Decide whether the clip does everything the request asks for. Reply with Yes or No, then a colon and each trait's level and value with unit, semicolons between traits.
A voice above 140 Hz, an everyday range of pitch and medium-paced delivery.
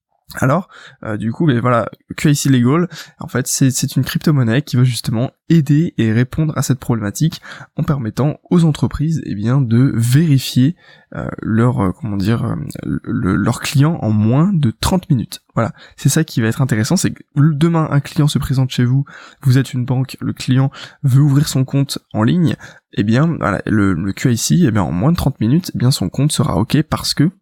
No: low, 135 Hz; average, 4.4 semitones; average, 205 wpm